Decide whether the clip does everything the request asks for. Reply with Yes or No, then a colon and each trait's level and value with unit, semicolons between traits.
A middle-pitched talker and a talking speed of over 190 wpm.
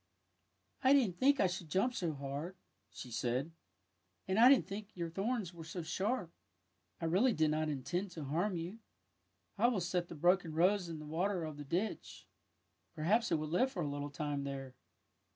Yes: medium, 170 Hz; average, 200 wpm